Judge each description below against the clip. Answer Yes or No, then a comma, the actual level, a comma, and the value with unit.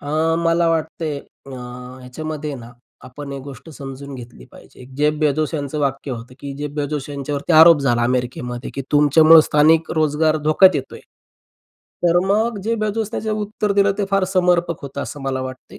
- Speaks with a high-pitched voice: No, medium, 150 Hz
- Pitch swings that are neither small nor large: Yes, average, 3.4 semitones